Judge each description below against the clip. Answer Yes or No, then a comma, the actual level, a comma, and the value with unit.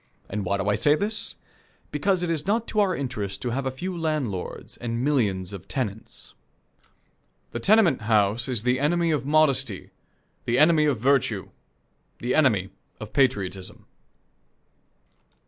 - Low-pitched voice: Yes, low, 130 Hz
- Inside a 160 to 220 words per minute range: No, average, 145 wpm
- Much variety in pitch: Yes, wide, 6.6 semitones